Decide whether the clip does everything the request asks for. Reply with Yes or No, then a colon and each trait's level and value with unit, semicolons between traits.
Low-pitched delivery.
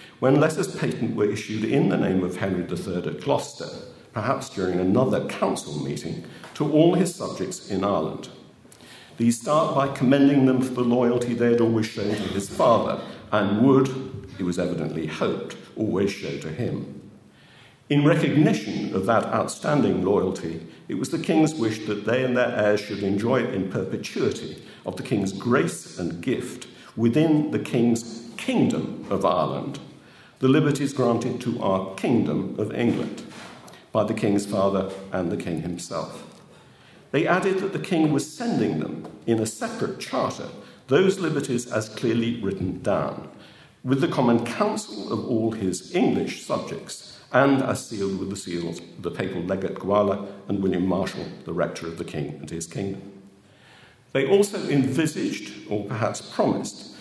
Yes: low, 115 Hz